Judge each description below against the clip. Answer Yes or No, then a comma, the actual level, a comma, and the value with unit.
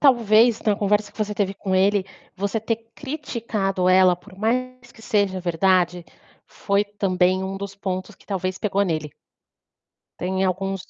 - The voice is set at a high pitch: Yes, high, 195 Hz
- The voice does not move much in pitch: Yes, narrow, 2.3 semitones